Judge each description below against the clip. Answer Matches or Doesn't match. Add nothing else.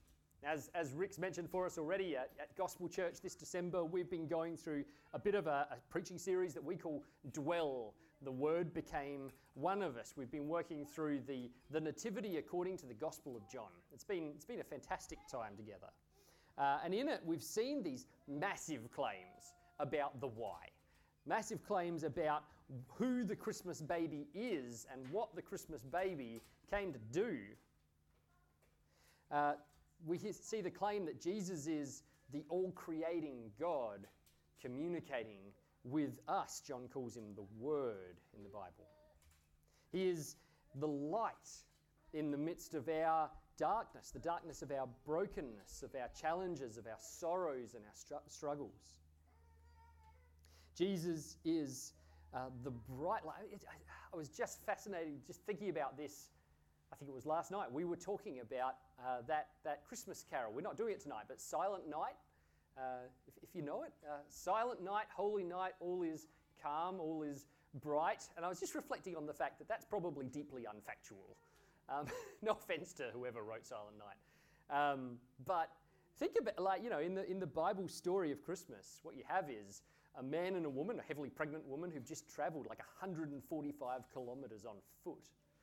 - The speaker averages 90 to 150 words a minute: Doesn't match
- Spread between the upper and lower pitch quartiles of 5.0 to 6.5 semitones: Matches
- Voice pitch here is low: Doesn't match